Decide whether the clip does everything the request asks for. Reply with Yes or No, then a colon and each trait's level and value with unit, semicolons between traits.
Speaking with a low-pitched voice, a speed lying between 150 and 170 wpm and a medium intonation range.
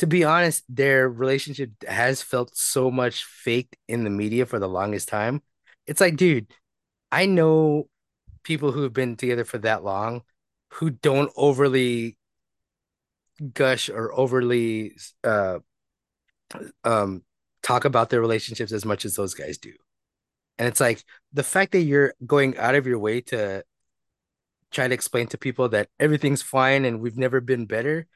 Yes: low, 130 Hz; average, 160 wpm; average, 3.7 semitones